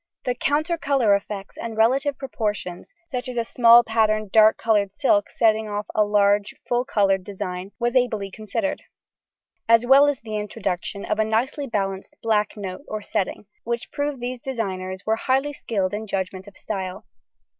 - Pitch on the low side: No, high, 220 Hz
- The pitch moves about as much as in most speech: Yes, average, 3.5 semitones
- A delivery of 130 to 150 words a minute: No, average, 165 wpm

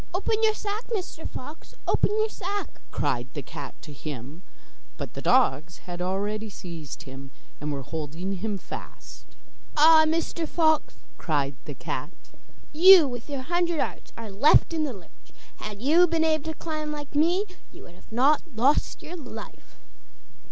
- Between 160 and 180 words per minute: Yes, average, 165 wpm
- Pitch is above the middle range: Yes, very high, 265 Hz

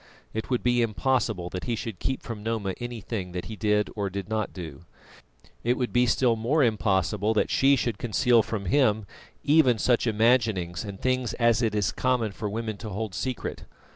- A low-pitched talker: Yes, low, 110 Hz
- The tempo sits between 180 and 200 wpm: Yes, average, 190 wpm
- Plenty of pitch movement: No, average, 3.0 semitones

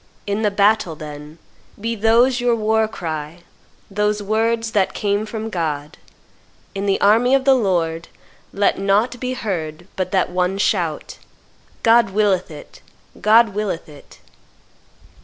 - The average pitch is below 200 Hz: No, high, 205 Hz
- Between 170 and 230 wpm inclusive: No, average, 140 wpm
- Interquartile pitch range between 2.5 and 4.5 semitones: Yes, average, 4.1 semitones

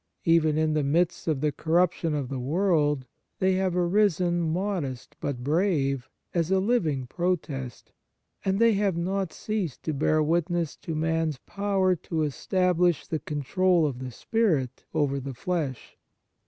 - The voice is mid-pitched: Yes, medium, 165 Hz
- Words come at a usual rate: Yes, average, 150 wpm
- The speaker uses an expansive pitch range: No, average, 4.0 semitones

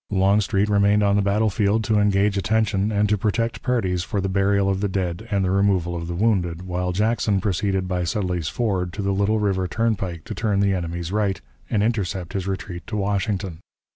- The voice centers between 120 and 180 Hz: No, low, 100 Hz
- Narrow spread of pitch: Yes, narrow, 2.2 semitones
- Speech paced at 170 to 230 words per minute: Yes, average, 200 wpm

